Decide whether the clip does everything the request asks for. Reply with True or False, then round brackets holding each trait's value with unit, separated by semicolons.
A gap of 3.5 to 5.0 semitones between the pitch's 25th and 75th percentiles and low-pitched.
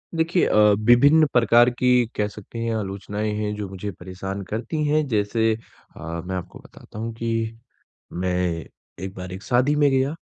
True (4.0 semitones; 110 Hz)